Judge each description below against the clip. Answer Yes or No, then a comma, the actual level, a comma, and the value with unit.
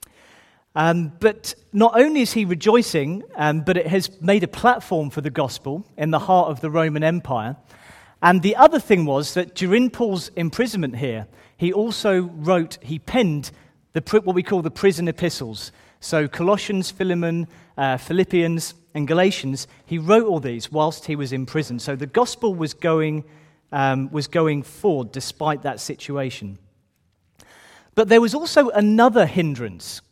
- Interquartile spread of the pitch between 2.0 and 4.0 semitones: No, wide, 5.4 semitones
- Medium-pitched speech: Yes, medium, 165 Hz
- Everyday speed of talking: Yes, average, 160 wpm